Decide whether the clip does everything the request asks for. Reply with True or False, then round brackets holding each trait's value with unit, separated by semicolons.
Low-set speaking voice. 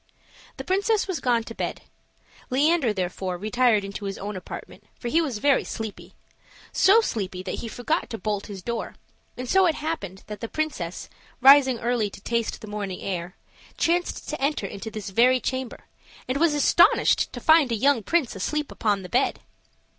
False (235 Hz)